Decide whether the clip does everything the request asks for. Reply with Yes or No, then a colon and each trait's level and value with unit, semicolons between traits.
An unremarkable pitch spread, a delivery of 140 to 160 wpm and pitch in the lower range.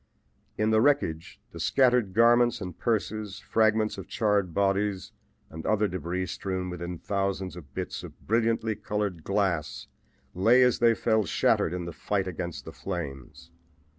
Yes: average, 3.7 semitones; average, 150 wpm; low, 100 Hz